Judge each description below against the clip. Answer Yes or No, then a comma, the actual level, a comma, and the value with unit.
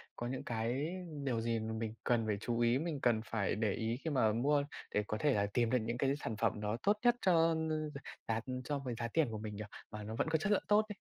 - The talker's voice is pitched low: Yes, low, 120 Hz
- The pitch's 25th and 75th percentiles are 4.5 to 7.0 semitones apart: Yes, average, 5.0 semitones